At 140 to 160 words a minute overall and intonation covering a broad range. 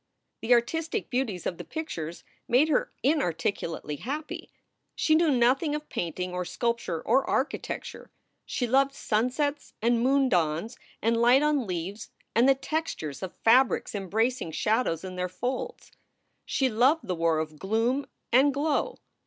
Yes: average, 155 wpm; wide, 7.1 semitones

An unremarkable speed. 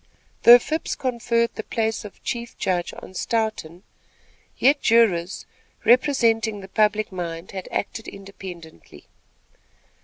No: slow, 110 wpm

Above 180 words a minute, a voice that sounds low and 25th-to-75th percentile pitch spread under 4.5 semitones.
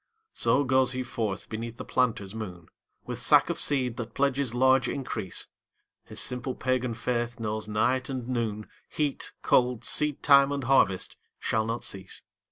No: average, 155 wpm; low, 125 Hz; average, 3.0 semitones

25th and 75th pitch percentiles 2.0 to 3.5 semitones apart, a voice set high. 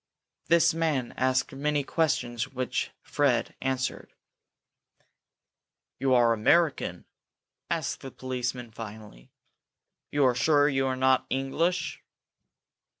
No: average, 2.9 semitones; low, 130 Hz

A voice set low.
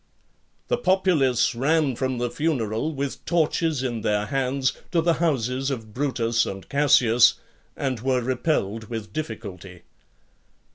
Yes: low, 130 Hz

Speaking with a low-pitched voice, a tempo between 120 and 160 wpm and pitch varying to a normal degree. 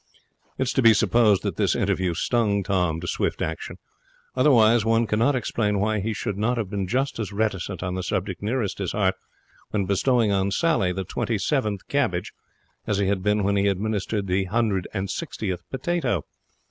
No: low, 105 Hz; average, 185 wpm; average, 3.2 semitones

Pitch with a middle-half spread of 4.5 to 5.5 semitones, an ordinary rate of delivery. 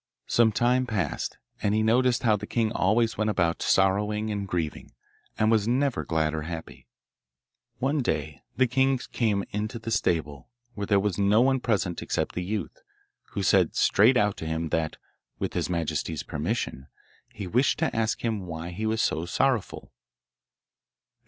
Yes: average, 5.0 semitones; average, 165 wpm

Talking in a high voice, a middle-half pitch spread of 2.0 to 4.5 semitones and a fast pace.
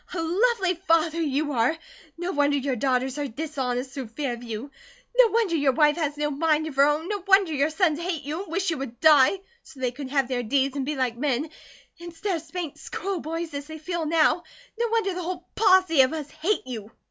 Yes: very high, 305 Hz; average, 4.1 semitones; fast, 225 wpm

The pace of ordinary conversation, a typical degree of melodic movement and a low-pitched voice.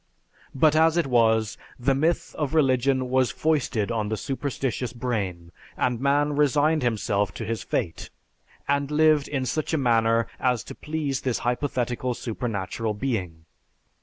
Yes: average, 145 wpm; average, 4.0 semitones; low, 130 Hz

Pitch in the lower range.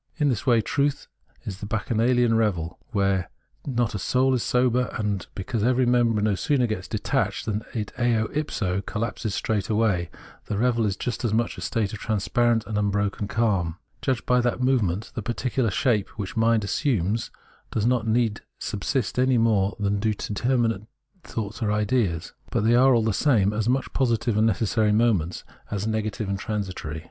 Yes: low, 110 Hz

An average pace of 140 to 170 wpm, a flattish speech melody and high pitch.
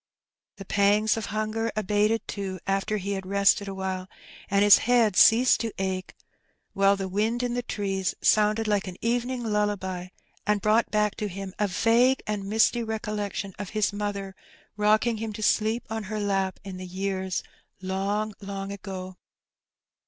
Yes: average, 160 wpm; narrow, 1.9 semitones; high, 205 Hz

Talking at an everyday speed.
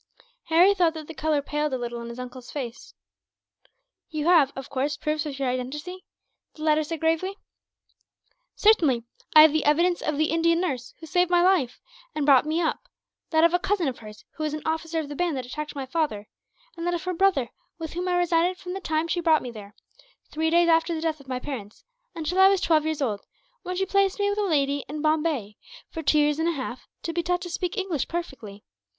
No: fast, 230 wpm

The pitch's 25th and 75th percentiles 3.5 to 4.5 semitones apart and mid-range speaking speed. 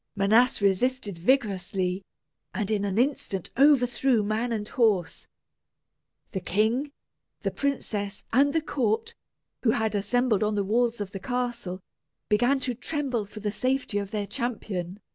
Yes: average, 3.8 semitones; average, 145 wpm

